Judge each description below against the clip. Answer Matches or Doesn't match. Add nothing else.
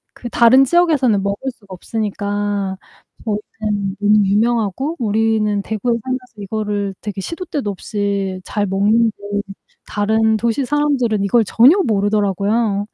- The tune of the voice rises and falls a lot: Doesn't match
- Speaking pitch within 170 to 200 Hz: Doesn't match